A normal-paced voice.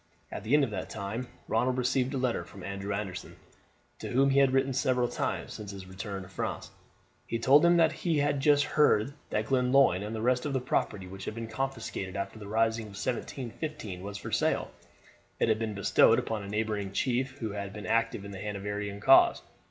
No: fast, 210 wpm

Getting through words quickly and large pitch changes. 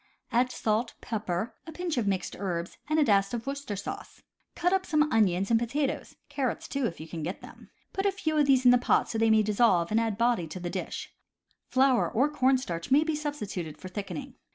Yes: fast, 235 wpm; wide, 6.1 semitones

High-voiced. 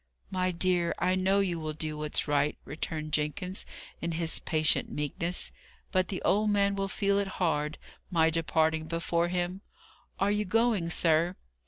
No: medium, 170 Hz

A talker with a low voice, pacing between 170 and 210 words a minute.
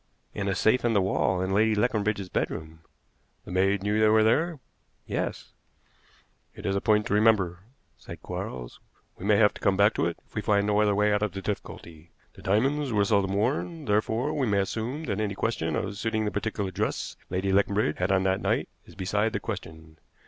Yes: low, 105 Hz; fast, 205 wpm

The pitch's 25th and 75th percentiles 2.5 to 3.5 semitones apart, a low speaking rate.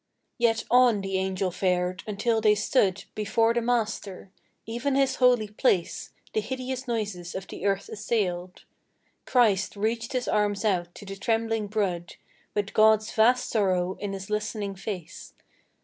No: average, 2.9 semitones; average, 150 wpm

